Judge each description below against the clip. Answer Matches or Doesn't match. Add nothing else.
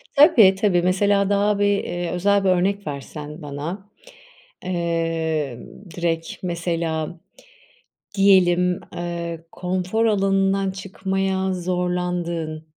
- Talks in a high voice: Doesn't match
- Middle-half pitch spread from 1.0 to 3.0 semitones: Matches